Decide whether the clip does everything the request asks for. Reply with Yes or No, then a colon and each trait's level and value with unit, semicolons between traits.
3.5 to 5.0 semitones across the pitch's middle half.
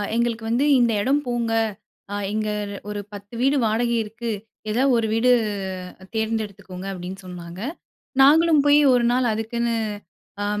No: average, 2.9 semitones